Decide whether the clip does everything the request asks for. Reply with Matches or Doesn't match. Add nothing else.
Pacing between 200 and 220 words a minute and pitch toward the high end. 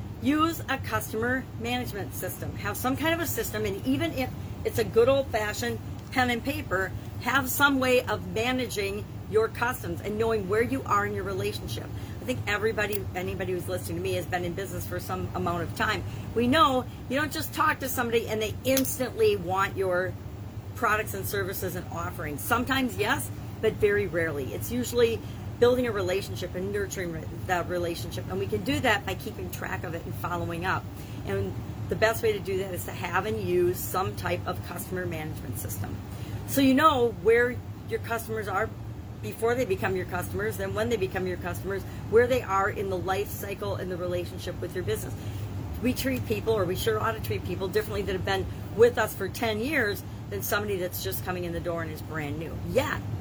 Doesn't match